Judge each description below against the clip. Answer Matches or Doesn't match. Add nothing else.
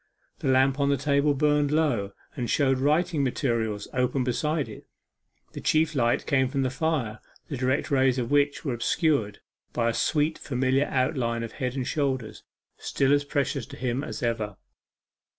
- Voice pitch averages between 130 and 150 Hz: Matches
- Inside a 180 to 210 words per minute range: Doesn't match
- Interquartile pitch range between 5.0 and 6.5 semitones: Doesn't match